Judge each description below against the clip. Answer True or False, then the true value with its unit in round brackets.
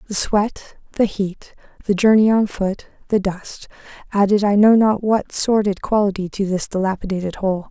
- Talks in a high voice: True (200 Hz)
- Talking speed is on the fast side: False (165 wpm)